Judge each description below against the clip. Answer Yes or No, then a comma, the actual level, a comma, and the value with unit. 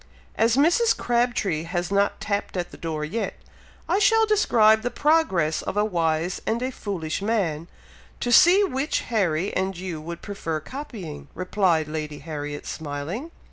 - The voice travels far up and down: Yes, wide, 7.1 semitones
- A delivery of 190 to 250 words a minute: No, average, 155 wpm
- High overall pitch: Yes, high, 195 Hz